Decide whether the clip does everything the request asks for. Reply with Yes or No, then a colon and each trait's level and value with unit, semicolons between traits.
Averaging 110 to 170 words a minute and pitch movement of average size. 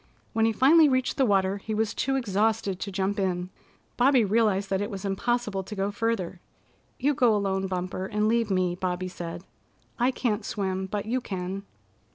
No: average, 185 wpm; average, 3.2 semitones